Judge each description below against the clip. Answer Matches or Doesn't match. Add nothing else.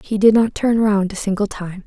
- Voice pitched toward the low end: Doesn't match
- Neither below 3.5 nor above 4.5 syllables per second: Doesn't match